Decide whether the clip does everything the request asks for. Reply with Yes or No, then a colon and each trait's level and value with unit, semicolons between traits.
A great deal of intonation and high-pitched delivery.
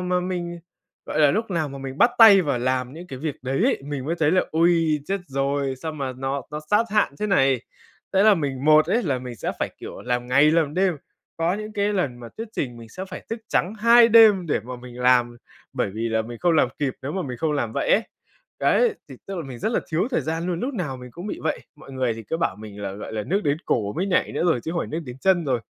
No: wide, 6.2 semitones; medium, 155 Hz